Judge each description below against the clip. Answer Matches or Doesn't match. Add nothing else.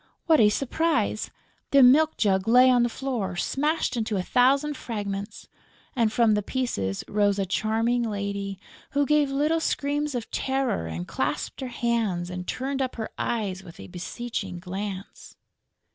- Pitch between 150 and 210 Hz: Doesn't match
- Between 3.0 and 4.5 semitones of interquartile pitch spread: Doesn't match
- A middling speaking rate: Matches